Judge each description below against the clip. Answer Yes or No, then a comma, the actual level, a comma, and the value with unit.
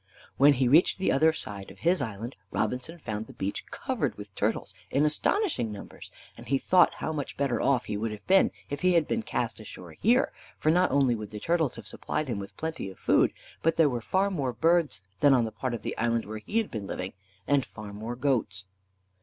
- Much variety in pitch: Yes, wide, 6.7 semitones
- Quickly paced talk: Yes, fast, 225 wpm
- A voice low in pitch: Yes, low, 130 Hz